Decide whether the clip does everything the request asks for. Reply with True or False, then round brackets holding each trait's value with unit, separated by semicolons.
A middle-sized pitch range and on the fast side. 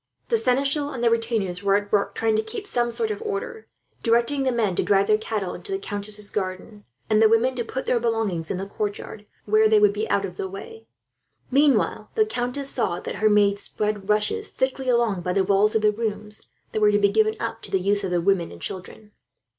True (3.2 semitones; 235 wpm)